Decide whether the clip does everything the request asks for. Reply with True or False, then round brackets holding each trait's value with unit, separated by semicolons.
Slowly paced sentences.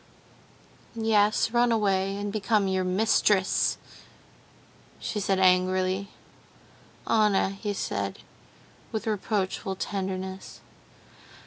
True (85 wpm)